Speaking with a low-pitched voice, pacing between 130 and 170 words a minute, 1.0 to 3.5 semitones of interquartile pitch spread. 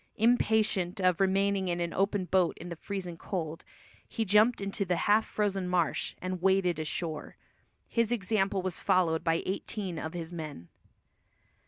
No: medium, 185 Hz; average, 155 wpm; average, 2.7 semitones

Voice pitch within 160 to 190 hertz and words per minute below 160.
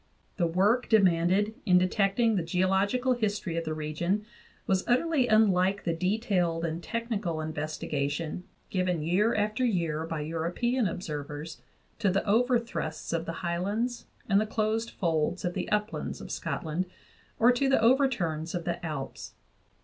Yes: medium, 185 Hz; average, 145 wpm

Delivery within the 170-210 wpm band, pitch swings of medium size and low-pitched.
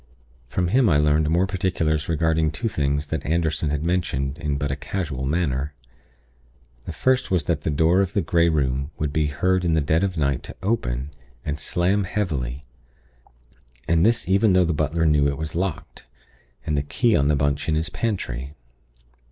Yes: average, 185 wpm; average, 3.8 semitones; very low, 80 Hz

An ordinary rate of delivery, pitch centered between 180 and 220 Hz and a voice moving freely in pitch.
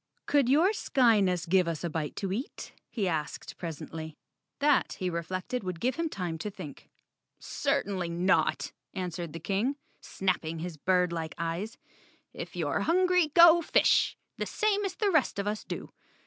Yes: average, 160 wpm; high, 190 Hz; wide, 8.0 semitones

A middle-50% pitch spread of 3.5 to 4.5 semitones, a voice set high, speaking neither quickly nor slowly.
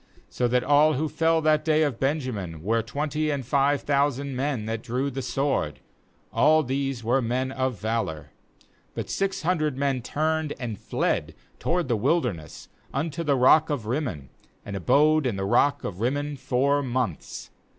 No: average, 4.1 semitones; low, 135 Hz; average, 165 wpm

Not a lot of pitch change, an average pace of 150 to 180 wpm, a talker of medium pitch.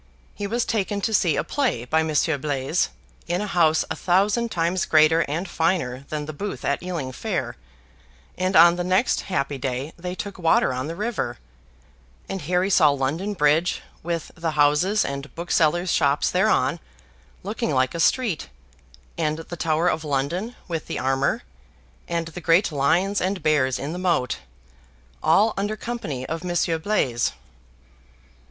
No: average, 4.2 semitones; average, 160 wpm; medium, 165 Hz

